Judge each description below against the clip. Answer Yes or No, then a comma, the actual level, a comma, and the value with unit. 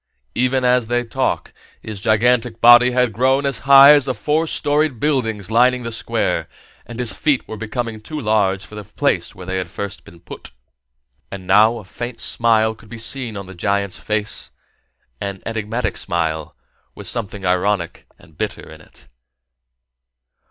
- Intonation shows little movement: No, average, 3.8 semitones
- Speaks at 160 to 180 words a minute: Yes, average, 165 wpm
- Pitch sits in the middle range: No, low, 110 Hz